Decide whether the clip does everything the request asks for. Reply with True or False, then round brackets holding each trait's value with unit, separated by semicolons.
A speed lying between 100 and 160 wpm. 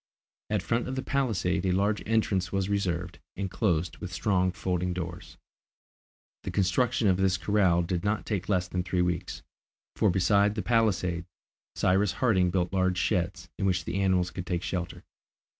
False (175 wpm)